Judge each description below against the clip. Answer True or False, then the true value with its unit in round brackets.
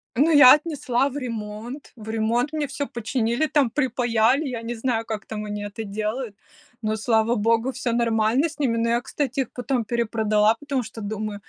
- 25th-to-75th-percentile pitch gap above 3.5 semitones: False (3.1 semitones)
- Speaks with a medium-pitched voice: False (235 Hz)